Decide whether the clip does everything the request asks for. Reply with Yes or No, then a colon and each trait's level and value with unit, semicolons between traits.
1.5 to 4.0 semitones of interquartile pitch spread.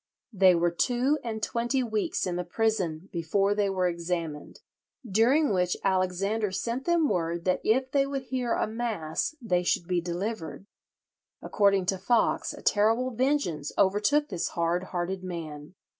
No: average, 5.0 semitones